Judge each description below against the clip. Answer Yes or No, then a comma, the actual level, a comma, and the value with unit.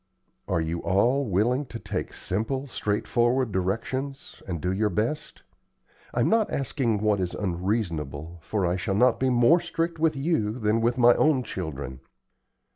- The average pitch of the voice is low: Yes, low, 110 Hz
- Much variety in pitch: Yes, wide, 5.9 semitones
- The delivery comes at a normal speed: Yes, average, 155 wpm